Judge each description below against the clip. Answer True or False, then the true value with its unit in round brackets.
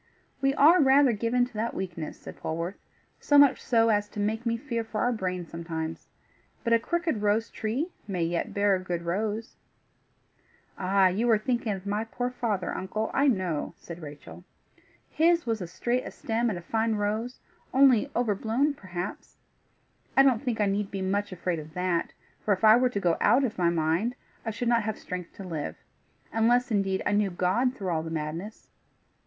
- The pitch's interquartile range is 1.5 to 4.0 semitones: False (4.6 semitones)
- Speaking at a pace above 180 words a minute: True (190 wpm)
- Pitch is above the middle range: True (210 Hz)